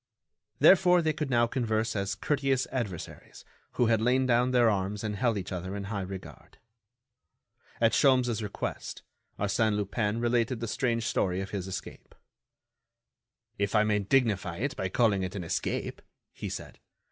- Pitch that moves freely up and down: No, average, 3.8 semitones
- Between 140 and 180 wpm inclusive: Yes, average, 160 wpm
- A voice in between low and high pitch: No, low, 110 Hz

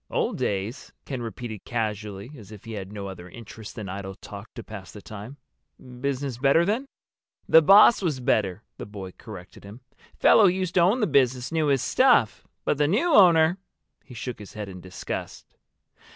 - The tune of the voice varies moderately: No, wide, 7.6 semitones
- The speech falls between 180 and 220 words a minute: Yes, average, 185 wpm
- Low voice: Yes, low, 120 Hz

